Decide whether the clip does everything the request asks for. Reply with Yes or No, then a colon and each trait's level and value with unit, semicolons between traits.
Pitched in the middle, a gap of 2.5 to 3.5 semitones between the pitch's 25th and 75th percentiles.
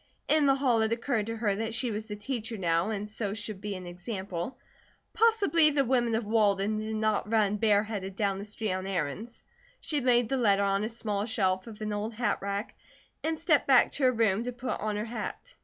No: high, 215 Hz; average, 3.0 semitones